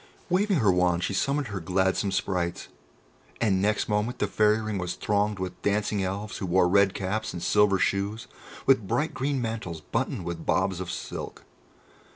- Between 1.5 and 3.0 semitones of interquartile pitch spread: Yes, average, 2.7 semitones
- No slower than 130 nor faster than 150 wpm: No, average, 175 wpm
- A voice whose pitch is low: Yes, low, 100 Hz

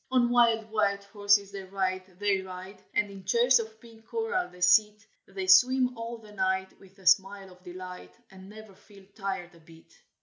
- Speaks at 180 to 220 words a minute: Yes, average, 190 wpm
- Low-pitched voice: No, high, 200 Hz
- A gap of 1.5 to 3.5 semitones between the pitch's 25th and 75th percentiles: Yes, average, 2.8 semitones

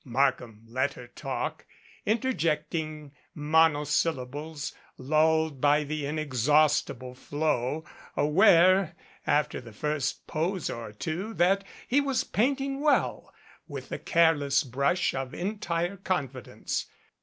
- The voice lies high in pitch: No, medium, 155 Hz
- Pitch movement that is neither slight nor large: Yes, average, 4.0 semitones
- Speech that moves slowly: Yes, slow, 105 wpm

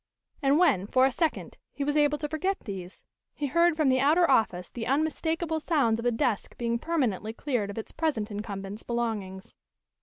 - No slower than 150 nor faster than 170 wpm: No, average, 185 wpm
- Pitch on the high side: Yes, very high, 255 Hz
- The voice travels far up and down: Yes, wide, 6.2 semitones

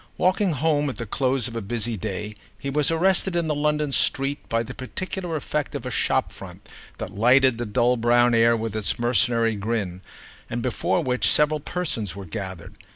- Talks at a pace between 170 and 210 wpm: Yes, average, 190 wpm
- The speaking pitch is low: Yes, low, 125 Hz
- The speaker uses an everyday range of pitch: Yes, average, 4.8 semitones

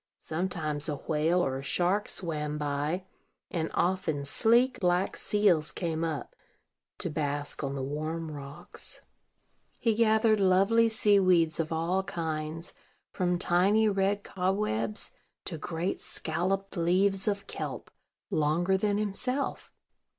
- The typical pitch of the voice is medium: Yes, medium, 175 Hz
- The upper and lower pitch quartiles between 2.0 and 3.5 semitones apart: No, average, 4.2 semitones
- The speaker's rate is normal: No, slow, 125 wpm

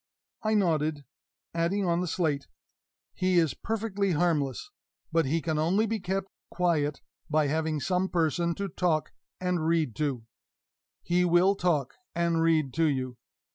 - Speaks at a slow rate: No, average, 145 wpm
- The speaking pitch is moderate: Yes, medium, 170 Hz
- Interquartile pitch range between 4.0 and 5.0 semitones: No, average, 2.8 semitones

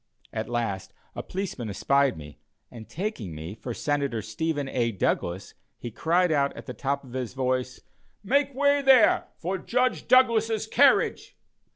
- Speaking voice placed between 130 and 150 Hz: Yes, medium, 140 Hz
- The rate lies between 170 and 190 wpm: No, average, 155 wpm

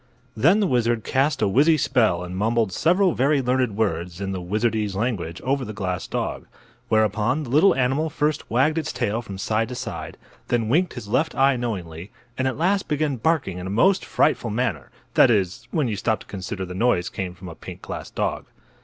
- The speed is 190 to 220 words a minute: Yes, average, 200 wpm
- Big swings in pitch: Yes, wide, 5.8 semitones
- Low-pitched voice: Yes, low, 115 Hz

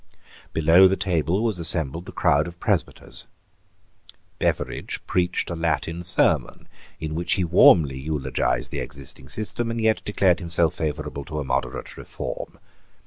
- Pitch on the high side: No, very low, 85 Hz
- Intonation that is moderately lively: Yes, average, 3.0 semitones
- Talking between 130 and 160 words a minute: Yes, average, 140 wpm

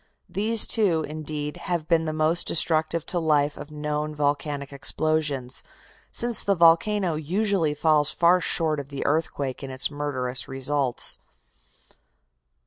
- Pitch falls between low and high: Yes, medium, 155 Hz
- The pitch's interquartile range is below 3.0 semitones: Yes, narrow, 2.5 semitones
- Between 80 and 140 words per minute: Yes, slow, 135 wpm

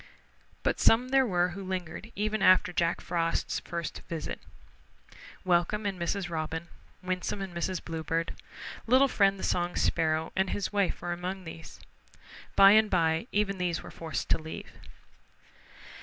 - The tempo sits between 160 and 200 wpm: No, average, 150 wpm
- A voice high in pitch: No, medium, 180 Hz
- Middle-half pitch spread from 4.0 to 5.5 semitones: No, average, 2.9 semitones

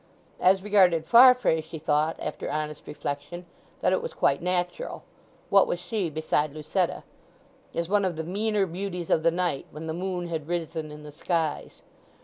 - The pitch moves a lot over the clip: No, average, 3.3 semitones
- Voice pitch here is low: No, medium, 170 Hz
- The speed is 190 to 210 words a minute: No, average, 165 wpm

